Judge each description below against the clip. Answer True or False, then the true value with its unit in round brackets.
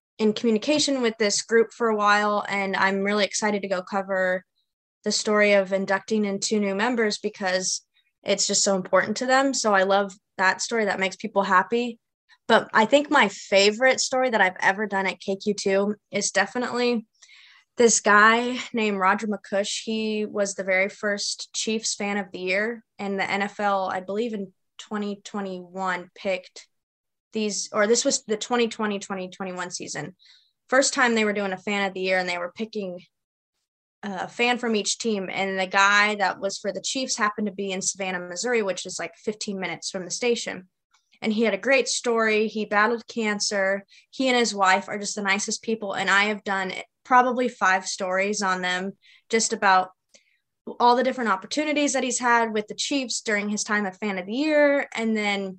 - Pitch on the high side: True (205 Hz)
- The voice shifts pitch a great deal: False (2.8 semitones)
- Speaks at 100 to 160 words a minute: False (190 wpm)